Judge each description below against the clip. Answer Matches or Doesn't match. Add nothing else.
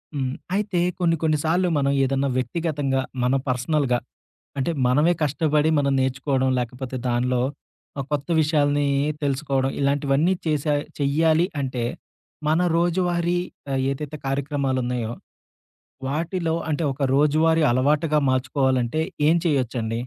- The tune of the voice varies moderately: Matches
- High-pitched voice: Doesn't match